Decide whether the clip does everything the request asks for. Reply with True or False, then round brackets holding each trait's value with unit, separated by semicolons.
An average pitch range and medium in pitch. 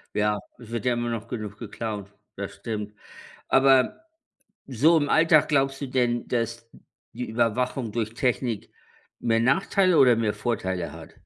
False (3.2 semitones; 120 Hz)